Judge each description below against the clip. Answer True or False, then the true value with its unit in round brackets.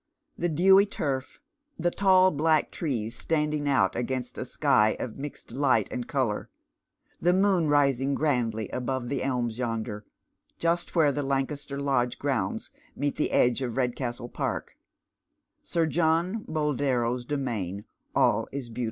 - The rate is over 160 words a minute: False (145 wpm)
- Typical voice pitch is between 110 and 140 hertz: True (135 Hz)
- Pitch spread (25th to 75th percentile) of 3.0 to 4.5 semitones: True (4.2 semitones)